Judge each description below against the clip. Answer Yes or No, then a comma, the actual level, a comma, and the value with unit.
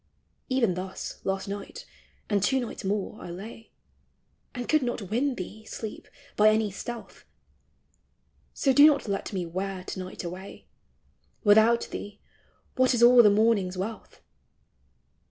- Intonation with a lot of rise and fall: No, average, 3.9 semitones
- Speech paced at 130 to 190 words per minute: Yes, average, 140 wpm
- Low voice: No, high, 210 Hz